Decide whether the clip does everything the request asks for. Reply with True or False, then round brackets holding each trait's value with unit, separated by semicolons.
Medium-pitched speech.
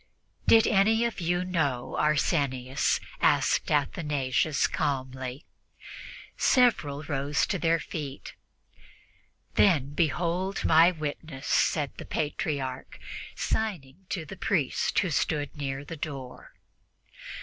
True (150 Hz)